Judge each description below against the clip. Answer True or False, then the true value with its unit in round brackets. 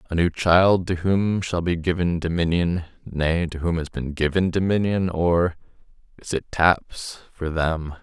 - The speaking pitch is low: True (85 Hz)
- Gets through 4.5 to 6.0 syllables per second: False (4.1 syllables/s)